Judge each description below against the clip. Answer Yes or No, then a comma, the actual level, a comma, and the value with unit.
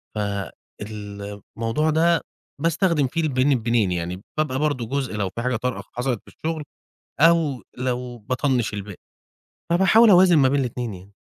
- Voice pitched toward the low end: Yes, low, 125 Hz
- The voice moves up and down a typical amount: No, wide, 6.4 semitones